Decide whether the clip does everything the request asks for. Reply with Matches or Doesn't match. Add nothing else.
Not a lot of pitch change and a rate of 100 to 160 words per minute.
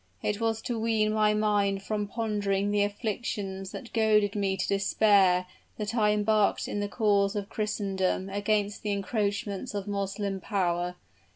Matches